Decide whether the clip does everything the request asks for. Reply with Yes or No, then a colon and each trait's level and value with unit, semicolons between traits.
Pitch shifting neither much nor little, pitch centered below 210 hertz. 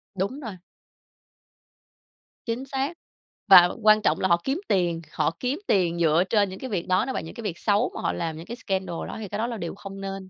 Yes: average, 4.7 semitones; high, 195 Hz